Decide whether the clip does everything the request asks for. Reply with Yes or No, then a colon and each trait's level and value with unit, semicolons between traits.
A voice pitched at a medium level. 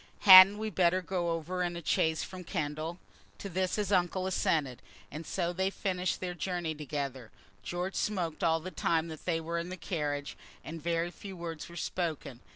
Yes: medium, 170 Hz